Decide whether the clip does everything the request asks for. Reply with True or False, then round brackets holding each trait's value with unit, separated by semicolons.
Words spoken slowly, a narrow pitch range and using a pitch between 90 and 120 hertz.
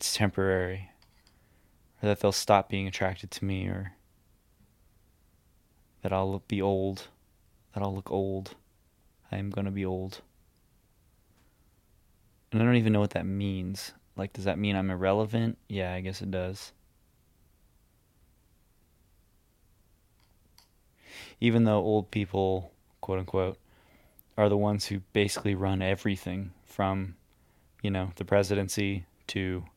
True (125 wpm; 1.7 semitones; 95 Hz)